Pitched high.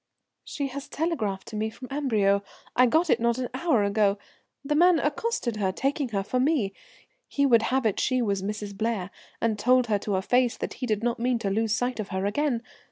Yes: high, 235 Hz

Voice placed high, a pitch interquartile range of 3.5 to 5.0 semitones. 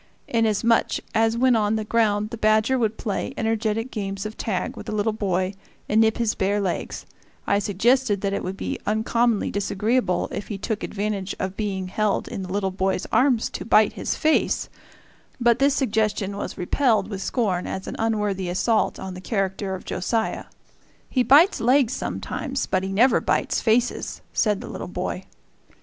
No: high, 215 Hz; average, 2.9 semitones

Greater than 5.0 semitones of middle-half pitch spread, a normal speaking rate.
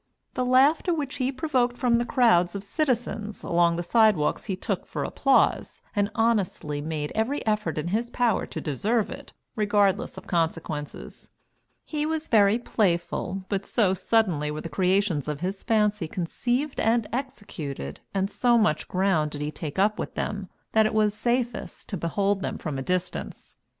Yes: wide, 5.6 semitones; average, 170 wpm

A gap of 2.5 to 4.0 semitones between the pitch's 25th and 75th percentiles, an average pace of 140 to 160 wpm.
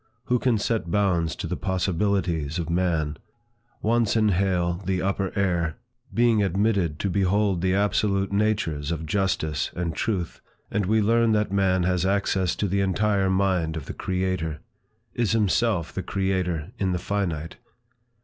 Yes: average, 2.9 semitones; average, 150 wpm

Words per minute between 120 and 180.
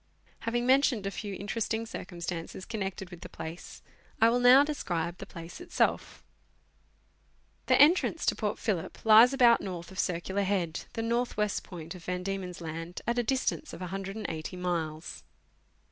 Yes: average, 160 wpm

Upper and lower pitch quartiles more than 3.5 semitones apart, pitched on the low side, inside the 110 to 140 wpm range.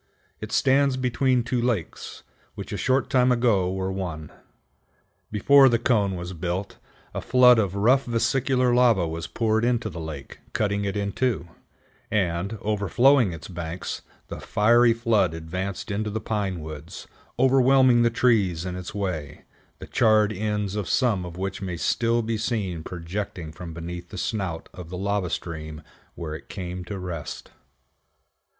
No: average, 5.0 semitones; low, 100 Hz; average, 155 wpm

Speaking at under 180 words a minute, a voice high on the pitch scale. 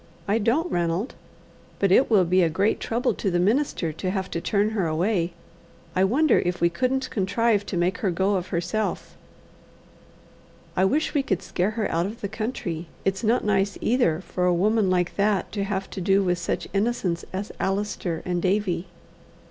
No: average, 190 wpm; high, 195 Hz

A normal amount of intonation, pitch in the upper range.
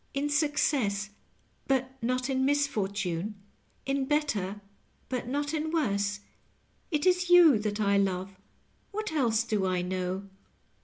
No: wide, 6.4 semitones; high, 240 Hz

